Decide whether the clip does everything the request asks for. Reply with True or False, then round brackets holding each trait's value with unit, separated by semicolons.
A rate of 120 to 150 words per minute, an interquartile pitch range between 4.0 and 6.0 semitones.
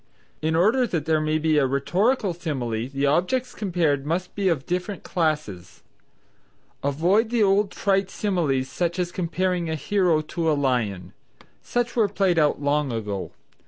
False (160 wpm; 5.2 semitones)